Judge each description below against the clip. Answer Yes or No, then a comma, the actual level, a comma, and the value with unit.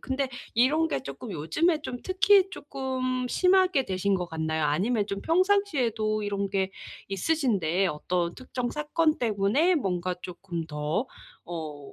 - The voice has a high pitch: Yes, high, 215 Hz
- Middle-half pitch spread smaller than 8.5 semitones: No, wide, 8.9 semitones